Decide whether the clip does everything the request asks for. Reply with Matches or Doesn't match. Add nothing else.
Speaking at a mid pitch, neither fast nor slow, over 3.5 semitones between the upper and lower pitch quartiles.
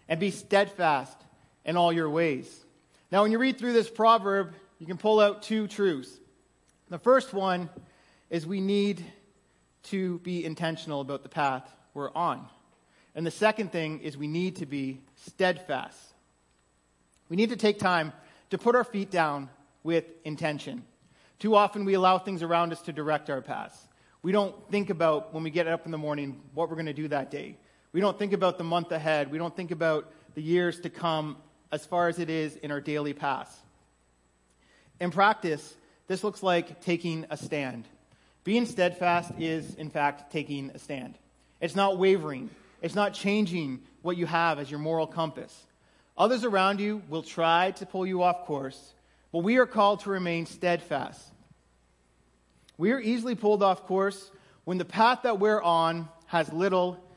Matches